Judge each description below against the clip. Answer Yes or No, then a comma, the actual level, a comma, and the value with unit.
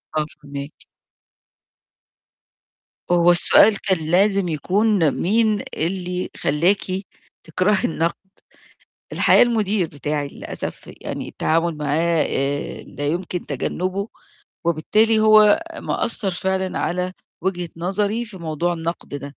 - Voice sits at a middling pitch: Yes, medium, 180 Hz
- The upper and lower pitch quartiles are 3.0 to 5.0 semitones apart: Yes, average, 4.0 semitones